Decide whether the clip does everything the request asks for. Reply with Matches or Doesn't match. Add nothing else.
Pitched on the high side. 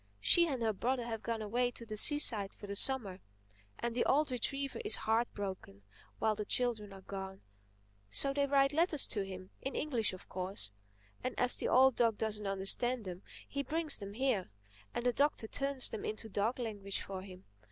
Matches